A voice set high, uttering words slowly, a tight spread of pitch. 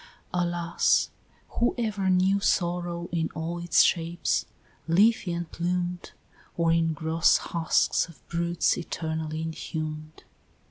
No: medium, 170 Hz; slow, 110 wpm; narrow, 1.5 semitones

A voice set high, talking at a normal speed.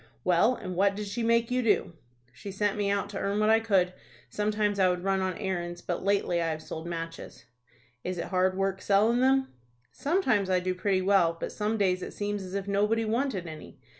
No: high, 195 Hz; fast, 215 wpm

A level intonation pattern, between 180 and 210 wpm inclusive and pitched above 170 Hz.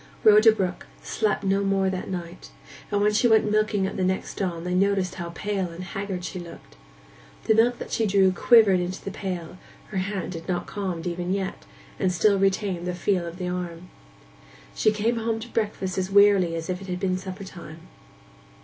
Yes: narrow, 2.2 semitones; average, 195 wpm; high, 190 Hz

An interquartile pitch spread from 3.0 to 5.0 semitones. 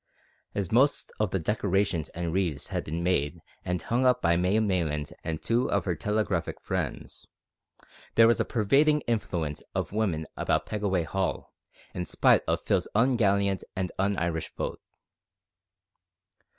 Yes: average, 4.2 semitones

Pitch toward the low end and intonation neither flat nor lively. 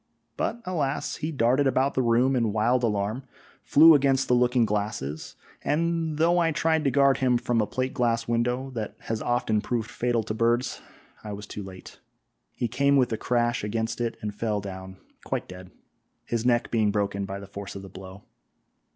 Yes: low, 120 Hz; average, 4.1 semitones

